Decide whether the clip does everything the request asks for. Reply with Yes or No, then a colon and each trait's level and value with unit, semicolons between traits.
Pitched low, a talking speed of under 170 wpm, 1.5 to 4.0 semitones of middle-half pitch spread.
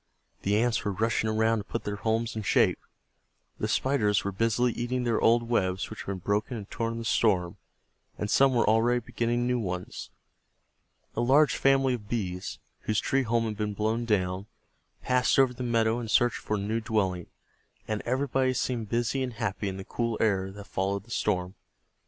No: low, 110 Hz; average, 195 wpm; average, 2.8 semitones